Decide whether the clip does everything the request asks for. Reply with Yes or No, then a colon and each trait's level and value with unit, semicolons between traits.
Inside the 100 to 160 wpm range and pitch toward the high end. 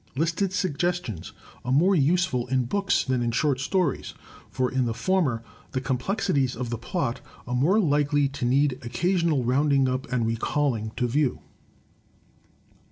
No: average, 150 wpm; low, 135 Hz